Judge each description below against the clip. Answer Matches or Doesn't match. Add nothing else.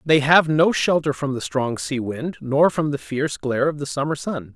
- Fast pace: Matches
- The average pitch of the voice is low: Doesn't match